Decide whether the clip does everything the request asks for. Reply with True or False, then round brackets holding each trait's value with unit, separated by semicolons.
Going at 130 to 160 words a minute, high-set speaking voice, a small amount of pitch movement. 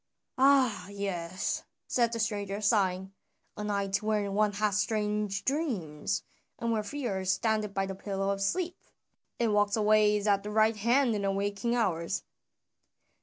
True (150 wpm; 210 Hz; 2.0 semitones)